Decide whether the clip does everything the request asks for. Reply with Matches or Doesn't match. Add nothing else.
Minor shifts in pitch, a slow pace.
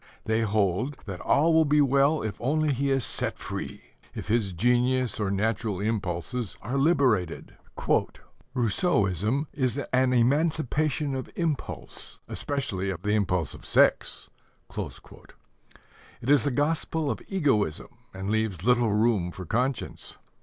Doesn't match